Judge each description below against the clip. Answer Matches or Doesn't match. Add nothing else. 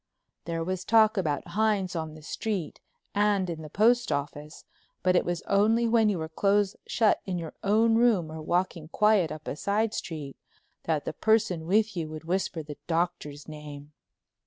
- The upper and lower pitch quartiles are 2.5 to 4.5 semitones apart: Doesn't match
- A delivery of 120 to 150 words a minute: Doesn't match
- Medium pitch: Matches